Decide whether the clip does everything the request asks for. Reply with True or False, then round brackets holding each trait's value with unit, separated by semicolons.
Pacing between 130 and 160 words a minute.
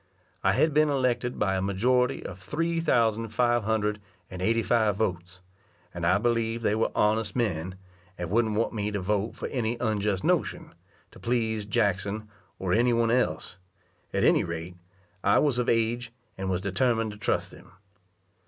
False (170 wpm)